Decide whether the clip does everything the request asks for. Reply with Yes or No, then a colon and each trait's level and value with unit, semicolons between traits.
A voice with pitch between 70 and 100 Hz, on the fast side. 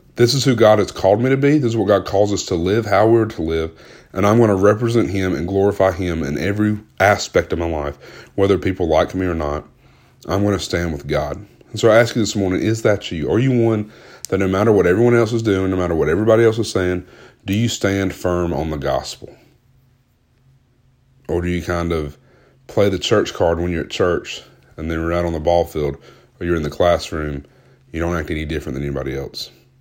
Yes: very low, 95 Hz; fast, 235 wpm